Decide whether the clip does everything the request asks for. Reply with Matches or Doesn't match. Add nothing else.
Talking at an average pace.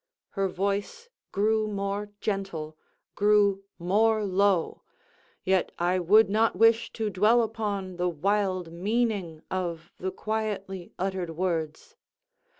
Doesn't match